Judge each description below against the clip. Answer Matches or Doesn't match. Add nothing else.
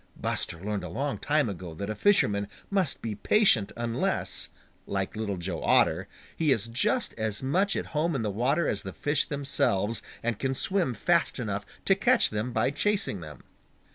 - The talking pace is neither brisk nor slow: Matches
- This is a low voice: Matches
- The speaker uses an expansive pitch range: Matches